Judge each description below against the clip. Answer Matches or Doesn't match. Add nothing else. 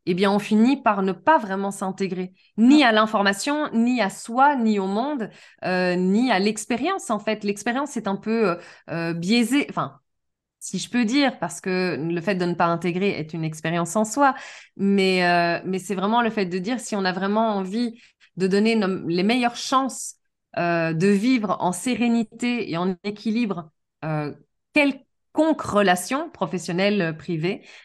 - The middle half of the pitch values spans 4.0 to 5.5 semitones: Matches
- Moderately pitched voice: Doesn't match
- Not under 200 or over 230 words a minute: Doesn't match